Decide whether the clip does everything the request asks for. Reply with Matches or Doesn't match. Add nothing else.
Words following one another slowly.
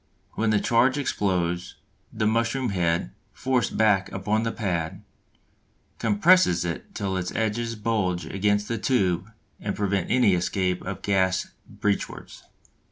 Matches